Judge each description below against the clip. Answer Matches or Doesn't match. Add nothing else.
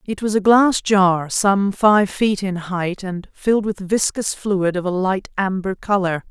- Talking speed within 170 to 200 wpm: Matches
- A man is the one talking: Doesn't match